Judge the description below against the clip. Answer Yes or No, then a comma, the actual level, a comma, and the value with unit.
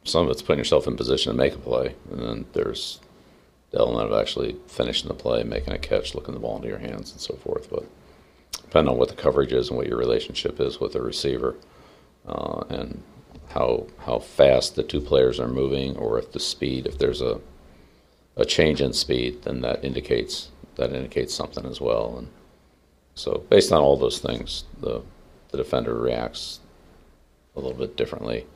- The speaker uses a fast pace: No, average, 195 wpm